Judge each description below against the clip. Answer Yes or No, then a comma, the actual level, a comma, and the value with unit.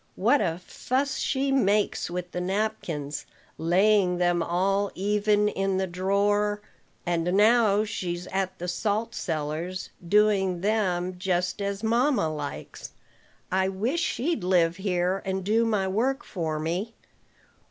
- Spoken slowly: Yes, slow, 130 wpm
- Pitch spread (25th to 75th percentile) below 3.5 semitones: Yes, average, 3.0 semitones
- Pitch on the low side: No, high, 190 Hz